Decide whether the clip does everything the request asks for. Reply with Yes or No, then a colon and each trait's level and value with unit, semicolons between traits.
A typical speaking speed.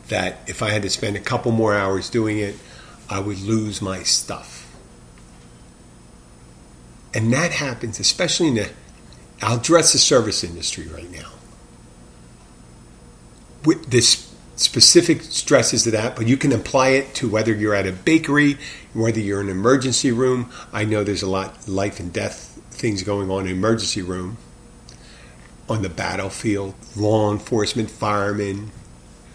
Yes: average, 150 wpm